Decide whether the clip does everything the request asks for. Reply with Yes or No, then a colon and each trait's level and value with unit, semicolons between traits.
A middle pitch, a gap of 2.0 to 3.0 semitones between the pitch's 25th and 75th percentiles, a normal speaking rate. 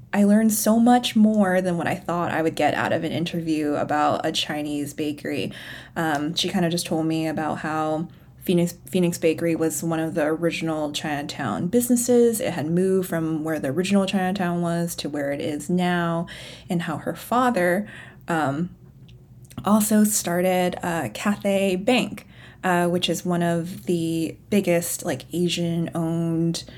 Yes: medium, 170 Hz; narrow, 2.6 semitones; average, 165 wpm